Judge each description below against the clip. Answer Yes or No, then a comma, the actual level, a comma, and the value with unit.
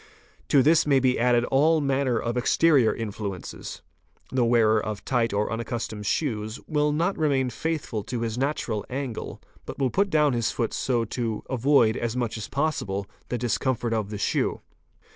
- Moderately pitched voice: No, low, 120 Hz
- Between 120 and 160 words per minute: No, average, 170 wpm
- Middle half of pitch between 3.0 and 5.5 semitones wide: Yes, average, 4.0 semitones